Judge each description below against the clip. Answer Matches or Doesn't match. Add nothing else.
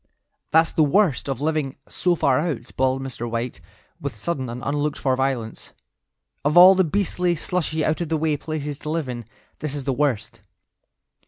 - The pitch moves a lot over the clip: Doesn't match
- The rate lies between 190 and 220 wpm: Doesn't match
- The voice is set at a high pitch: Doesn't match